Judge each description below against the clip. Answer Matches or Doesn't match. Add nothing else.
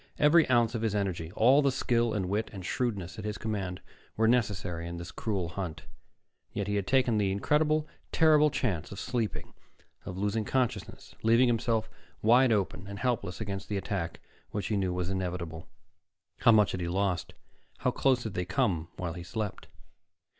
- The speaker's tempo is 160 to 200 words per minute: Matches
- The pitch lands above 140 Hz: Doesn't match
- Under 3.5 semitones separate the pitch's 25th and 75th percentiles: Doesn't match